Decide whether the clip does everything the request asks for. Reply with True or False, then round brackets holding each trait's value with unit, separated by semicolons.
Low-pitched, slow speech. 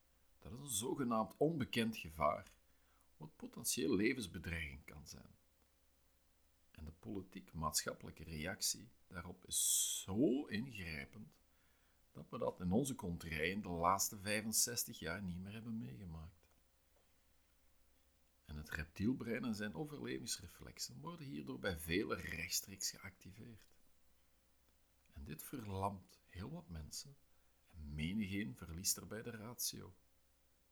True (85 Hz; 110 wpm)